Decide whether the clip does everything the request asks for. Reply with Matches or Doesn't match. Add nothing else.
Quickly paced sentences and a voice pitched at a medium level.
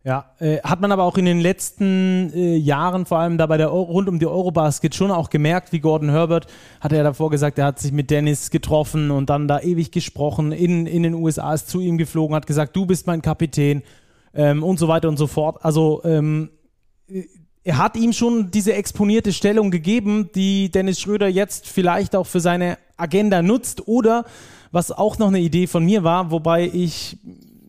Matches